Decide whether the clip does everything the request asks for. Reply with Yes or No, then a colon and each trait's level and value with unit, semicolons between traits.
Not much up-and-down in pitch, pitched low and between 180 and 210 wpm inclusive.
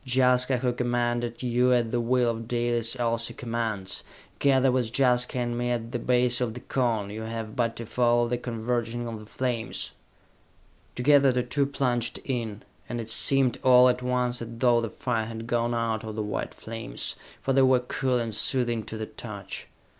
Yes: narrow, 1.5 semitones; low, 120 Hz; average, 190 wpm